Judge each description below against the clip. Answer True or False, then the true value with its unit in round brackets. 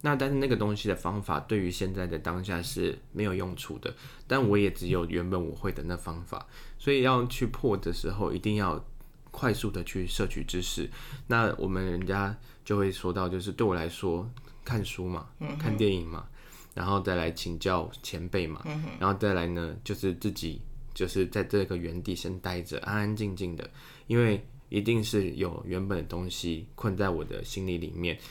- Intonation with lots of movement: False (4.7 semitones)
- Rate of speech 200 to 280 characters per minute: True (275 characters per minute)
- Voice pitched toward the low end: True (95 Hz)